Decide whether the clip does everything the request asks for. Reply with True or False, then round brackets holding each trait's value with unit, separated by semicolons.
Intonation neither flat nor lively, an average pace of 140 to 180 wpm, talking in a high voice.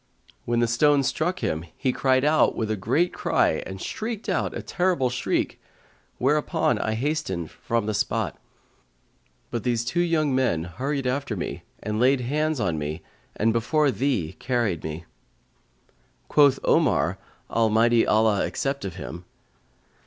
False (5.0 semitones; 145 wpm; 120 Hz)